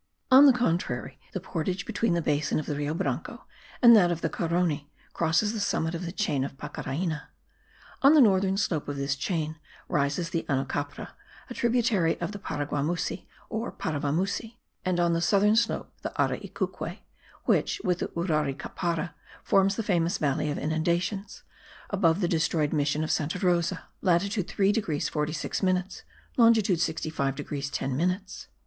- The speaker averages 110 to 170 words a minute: Yes, average, 160 wpm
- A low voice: No, medium, 170 Hz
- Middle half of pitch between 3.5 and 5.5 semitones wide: Yes, average, 4.5 semitones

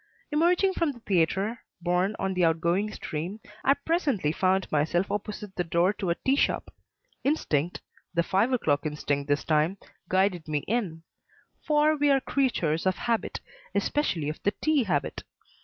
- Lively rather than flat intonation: Yes, wide, 7.7 semitones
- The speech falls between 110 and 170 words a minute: Yes, average, 155 wpm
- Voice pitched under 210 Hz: Yes, high, 190 Hz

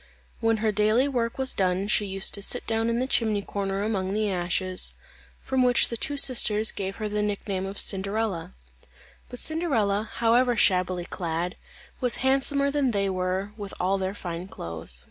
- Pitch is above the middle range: Yes, high, 205 Hz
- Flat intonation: No, average, 3.6 semitones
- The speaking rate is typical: Yes, average, 180 wpm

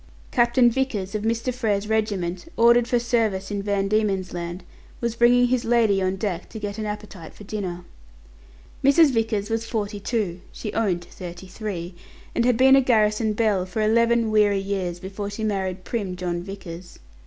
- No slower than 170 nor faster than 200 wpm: Yes, average, 175 wpm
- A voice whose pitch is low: No, high, 210 Hz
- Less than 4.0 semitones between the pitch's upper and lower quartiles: Yes, average, 3.4 semitones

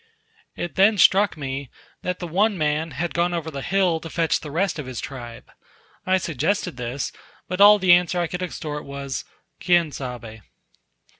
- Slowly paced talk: No, average, 175 wpm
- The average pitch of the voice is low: No, medium, 165 Hz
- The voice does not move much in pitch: No, average, 4.6 semitones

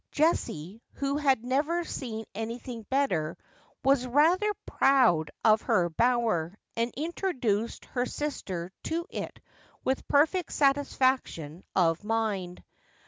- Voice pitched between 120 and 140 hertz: No, high, 245 Hz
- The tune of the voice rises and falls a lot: Yes, wide, 6.1 semitones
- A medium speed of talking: No, slow, 110 wpm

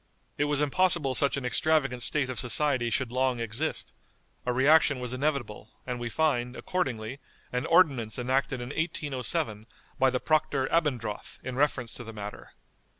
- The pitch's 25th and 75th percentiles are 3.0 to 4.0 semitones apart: Yes, average, 3.3 semitones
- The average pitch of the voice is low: Yes, low, 130 Hz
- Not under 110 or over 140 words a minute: No, average, 155 wpm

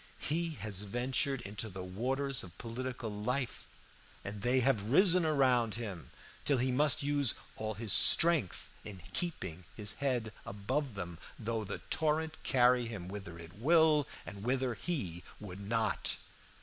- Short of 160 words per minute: Yes, average, 150 wpm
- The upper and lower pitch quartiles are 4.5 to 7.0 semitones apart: Yes, average, 5.2 semitones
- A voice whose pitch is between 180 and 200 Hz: No, low, 120 Hz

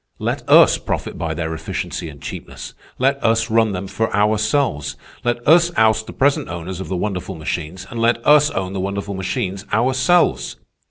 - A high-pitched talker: No, low, 105 Hz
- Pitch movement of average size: Yes, average, 4.8 semitones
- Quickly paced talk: No, average, 175 wpm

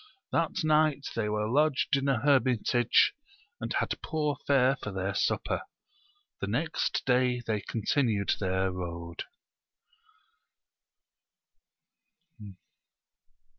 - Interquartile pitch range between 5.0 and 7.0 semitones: Yes, wide, 5.5 semitones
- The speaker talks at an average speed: No, slow, 95 wpm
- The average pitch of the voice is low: Yes, low, 125 Hz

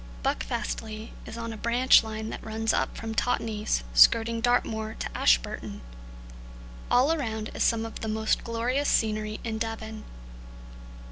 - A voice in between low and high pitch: No, high, 220 Hz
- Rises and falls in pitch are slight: Yes, narrow, 1.1 semitones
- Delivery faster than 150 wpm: No, average, 140 wpm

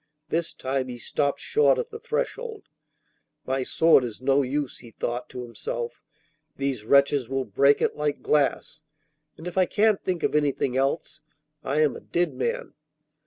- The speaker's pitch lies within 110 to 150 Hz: Yes, medium, 140 Hz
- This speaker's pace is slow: No, average, 165 wpm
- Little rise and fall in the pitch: No, average, 4.4 semitones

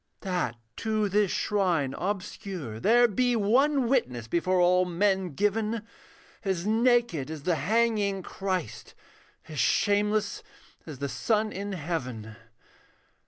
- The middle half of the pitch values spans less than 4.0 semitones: No, average, 4.3 semitones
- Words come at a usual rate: No, slow, 120 wpm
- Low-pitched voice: No, high, 195 Hz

